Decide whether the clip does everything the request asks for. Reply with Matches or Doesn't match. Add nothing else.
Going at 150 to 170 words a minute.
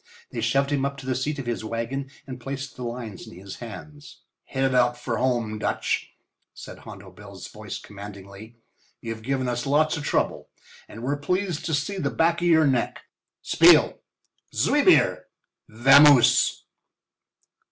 Matches